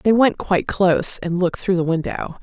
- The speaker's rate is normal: No, fast, 225 wpm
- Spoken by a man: No, female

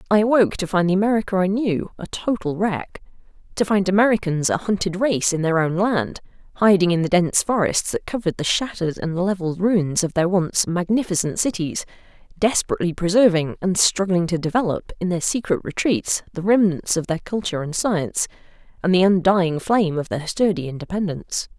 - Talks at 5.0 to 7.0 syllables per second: Yes, 5.7 syllables/s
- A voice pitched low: No, medium, 185 Hz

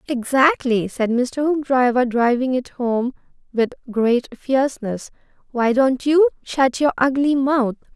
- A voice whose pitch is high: Yes, very high, 255 Hz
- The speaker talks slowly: Yes, slow, 130 wpm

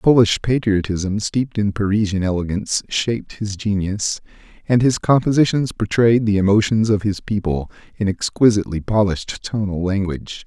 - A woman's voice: No, male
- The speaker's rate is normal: No, slow, 130 wpm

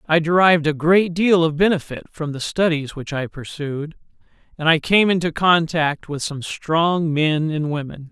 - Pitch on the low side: No, medium, 160 Hz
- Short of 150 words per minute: No, average, 175 wpm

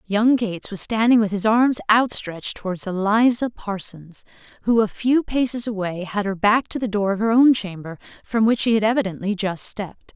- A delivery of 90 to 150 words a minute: No, average, 195 wpm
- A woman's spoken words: Yes, female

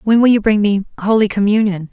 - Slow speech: No, fast, 220 wpm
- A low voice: No, high, 210 Hz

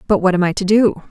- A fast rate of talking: Yes, fast, 325 wpm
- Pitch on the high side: Yes, high, 195 Hz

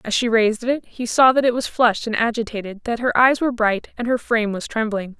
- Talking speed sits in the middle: No, fast, 255 wpm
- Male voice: No, female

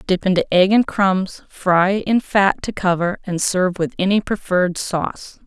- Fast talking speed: No, average, 175 wpm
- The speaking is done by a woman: Yes, female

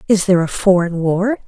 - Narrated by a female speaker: Yes, female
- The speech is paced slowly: No, fast, 205 wpm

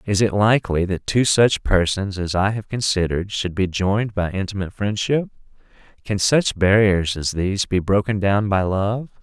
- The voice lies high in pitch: No, low, 100 Hz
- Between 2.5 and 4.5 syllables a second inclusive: No, 5.0 syllables/s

